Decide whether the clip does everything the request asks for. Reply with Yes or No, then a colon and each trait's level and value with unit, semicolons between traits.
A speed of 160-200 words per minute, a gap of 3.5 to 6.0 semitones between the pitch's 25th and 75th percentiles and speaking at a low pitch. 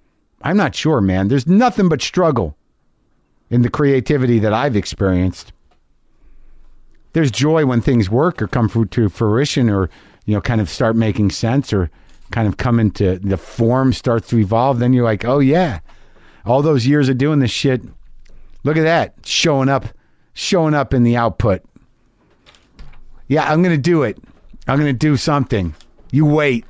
Yes: average, 165 wpm; average, 5.3 semitones; low, 120 Hz